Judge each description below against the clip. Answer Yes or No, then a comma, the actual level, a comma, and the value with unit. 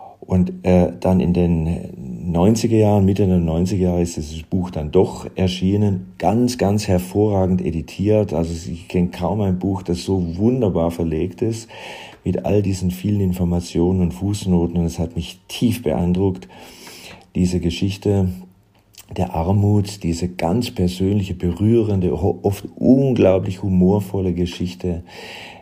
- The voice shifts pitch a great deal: No, narrow, 2.4 semitones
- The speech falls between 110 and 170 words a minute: Yes, average, 135 wpm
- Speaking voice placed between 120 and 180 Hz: No, very low, 90 Hz